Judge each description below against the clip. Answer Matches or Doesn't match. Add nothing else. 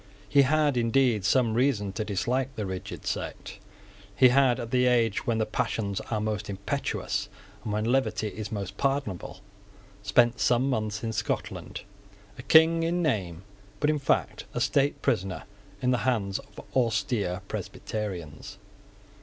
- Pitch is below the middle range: Matches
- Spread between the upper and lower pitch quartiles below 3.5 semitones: Doesn't match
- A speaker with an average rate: Matches